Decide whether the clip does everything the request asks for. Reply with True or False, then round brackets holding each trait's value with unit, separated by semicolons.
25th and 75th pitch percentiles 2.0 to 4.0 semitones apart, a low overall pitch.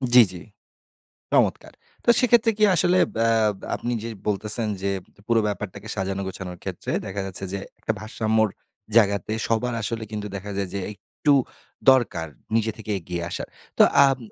True (3.1 semitones; 105 Hz)